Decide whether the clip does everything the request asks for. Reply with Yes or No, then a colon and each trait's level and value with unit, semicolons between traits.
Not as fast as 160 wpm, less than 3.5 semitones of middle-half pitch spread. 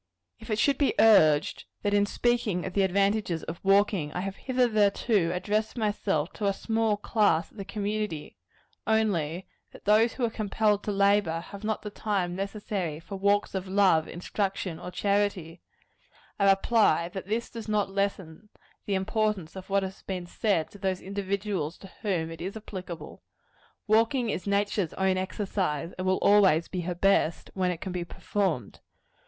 No: average, 170 wpm; average, 2.7 semitones